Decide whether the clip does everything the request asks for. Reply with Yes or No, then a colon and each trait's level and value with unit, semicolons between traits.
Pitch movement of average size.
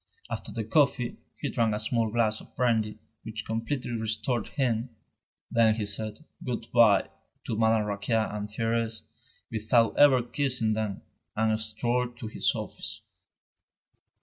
No: narrow, 1.6 semitones